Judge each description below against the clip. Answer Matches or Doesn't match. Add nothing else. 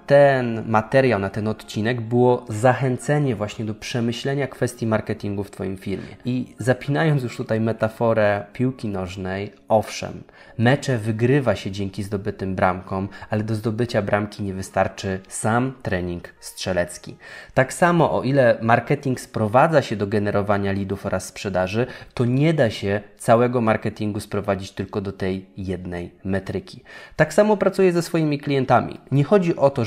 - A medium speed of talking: Matches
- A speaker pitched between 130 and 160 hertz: Doesn't match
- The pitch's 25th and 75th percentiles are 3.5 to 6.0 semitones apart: Matches